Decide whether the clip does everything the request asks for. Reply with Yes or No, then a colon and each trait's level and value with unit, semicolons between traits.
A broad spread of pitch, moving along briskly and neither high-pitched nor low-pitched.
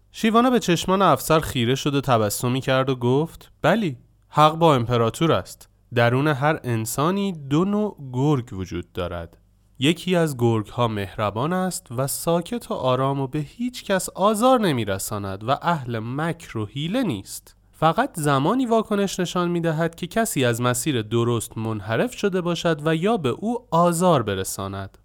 Yes: wide, 7.3 semitones; fast, 160 wpm; medium, 145 Hz